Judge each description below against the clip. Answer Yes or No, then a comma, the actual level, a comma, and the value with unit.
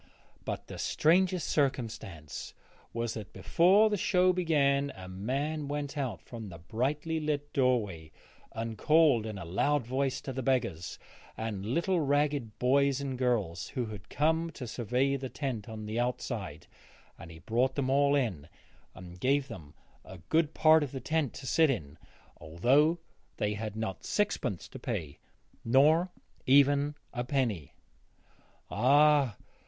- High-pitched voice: No, low, 130 Hz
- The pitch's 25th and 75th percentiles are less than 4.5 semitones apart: No, wide, 5.4 semitones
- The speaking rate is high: No, average, 150 wpm